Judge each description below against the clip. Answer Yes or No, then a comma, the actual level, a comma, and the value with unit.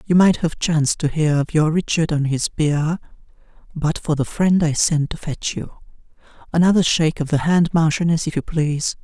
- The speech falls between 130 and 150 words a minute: No, average, 200 wpm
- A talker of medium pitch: Yes, medium, 160 Hz